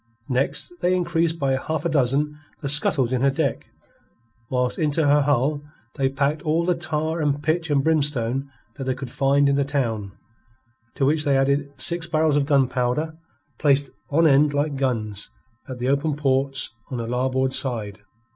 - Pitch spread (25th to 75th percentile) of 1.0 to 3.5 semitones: Yes, narrow, 2.6 semitones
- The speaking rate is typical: Yes, average, 175 wpm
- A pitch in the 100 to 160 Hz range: Yes, medium, 140 Hz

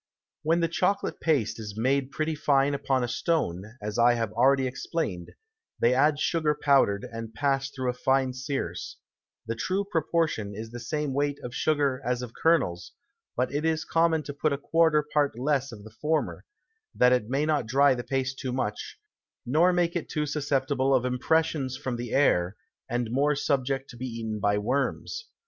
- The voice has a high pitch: No, low, 135 Hz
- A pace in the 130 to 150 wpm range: No, average, 185 wpm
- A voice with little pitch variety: No, average, 3.9 semitones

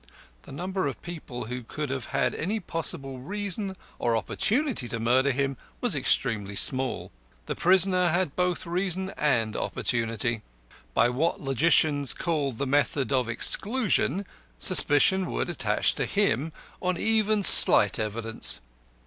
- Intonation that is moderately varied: No, wide, 6.9 semitones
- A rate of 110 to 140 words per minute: Yes, slow, 135 wpm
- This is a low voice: No, medium, 145 Hz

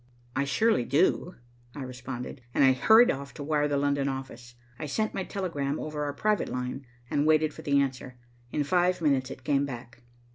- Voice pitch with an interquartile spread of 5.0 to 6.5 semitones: No, average, 2.9 semitones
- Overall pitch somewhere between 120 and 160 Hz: Yes, medium, 140 Hz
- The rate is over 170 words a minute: Yes, average, 190 wpm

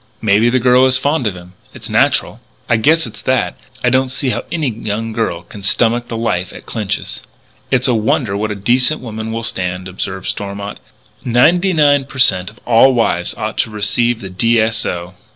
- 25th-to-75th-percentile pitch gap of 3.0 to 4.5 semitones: Yes, average, 4.0 semitones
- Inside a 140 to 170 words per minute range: No, fast, 205 wpm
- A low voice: Yes, low, 115 Hz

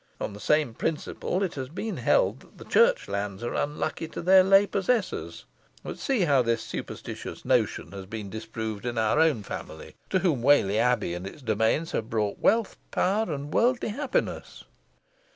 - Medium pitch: Yes, medium, 145 Hz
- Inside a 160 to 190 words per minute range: Yes, average, 170 wpm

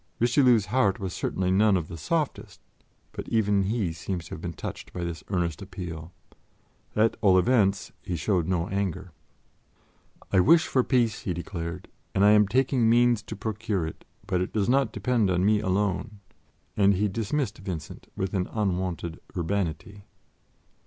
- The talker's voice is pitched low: Yes, low, 100 Hz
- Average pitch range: Yes, average, 3.5 semitones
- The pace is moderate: Yes, average, 165 wpm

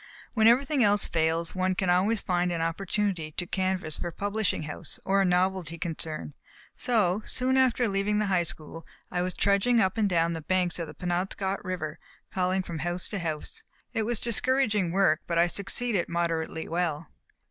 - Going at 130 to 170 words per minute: No, average, 180 wpm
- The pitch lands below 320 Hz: Yes, medium, 185 Hz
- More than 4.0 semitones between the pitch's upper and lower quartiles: No, average, 3.4 semitones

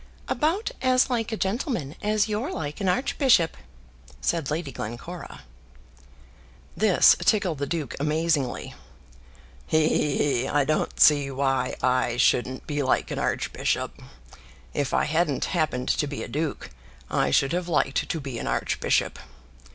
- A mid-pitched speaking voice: Yes, medium, 155 Hz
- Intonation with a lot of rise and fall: Yes, wide, 5.8 semitones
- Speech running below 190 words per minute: Yes, average, 145 wpm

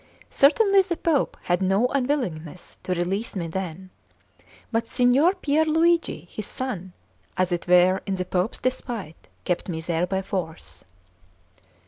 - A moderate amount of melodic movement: No, wide, 7.5 semitones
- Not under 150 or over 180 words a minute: No, average, 140 wpm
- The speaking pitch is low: No, high, 195 Hz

